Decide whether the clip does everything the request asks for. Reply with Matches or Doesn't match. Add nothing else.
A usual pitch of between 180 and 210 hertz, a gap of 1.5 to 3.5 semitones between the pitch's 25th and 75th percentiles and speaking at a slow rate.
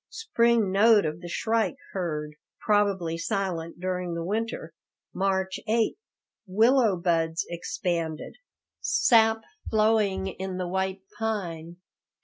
Doesn't match